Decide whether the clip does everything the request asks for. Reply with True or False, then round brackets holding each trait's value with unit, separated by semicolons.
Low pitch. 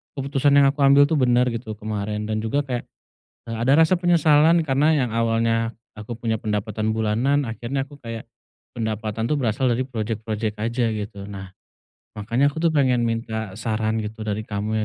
True (115 Hz)